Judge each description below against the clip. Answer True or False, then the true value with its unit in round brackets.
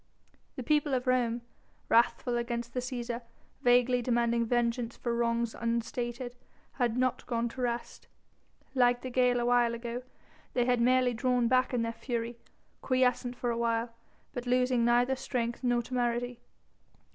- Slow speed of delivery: False (150 wpm)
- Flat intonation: True (1.1 semitones)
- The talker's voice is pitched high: True (245 Hz)